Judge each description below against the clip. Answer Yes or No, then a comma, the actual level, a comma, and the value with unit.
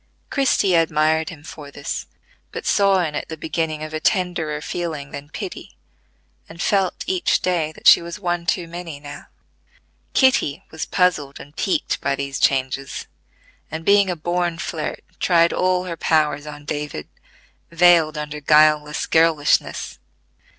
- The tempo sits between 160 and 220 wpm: No, average, 150 wpm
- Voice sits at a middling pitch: Yes, medium, 160 Hz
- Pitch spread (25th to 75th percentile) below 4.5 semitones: Yes, average, 2.9 semitones